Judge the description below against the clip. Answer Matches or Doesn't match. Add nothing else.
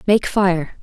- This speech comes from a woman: Matches